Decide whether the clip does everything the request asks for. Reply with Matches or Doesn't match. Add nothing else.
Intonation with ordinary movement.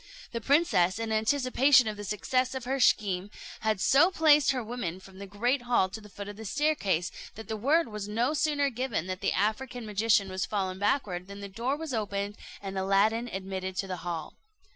Matches